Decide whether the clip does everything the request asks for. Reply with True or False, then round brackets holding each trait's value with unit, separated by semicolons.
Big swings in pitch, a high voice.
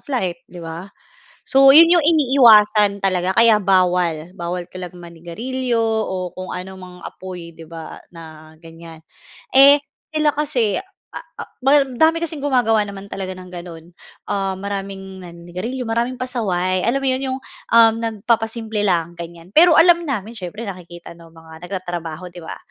True (5.8 semitones; 195 Hz)